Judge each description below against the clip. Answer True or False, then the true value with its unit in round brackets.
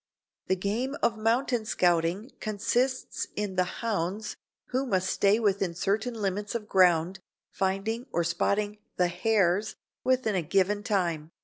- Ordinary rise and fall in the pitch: True (3.4 semitones)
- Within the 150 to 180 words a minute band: False (135 wpm)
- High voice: True (205 Hz)